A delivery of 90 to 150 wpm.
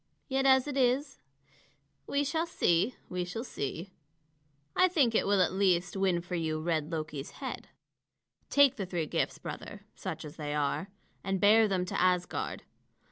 No: average, 165 wpm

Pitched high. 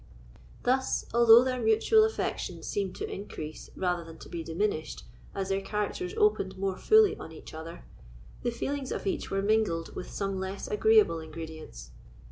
Yes: high, 195 Hz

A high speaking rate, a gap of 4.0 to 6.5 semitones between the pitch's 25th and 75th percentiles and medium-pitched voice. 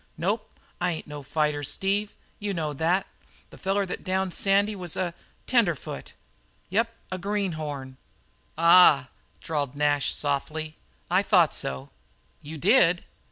No: average, 140 wpm; average, 4.8 semitones; medium, 170 Hz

